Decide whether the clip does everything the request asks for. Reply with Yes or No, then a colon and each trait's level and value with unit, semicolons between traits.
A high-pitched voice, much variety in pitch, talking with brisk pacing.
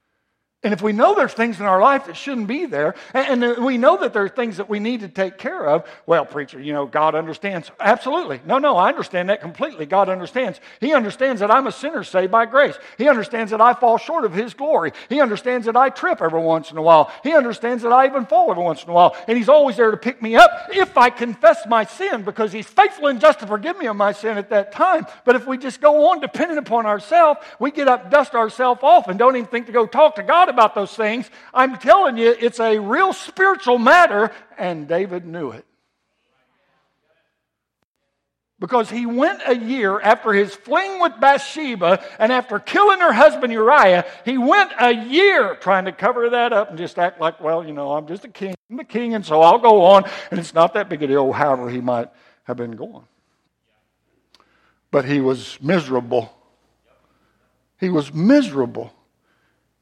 Yes: high, 230 Hz; wide, 6.5 semitones; fast, 210 wpm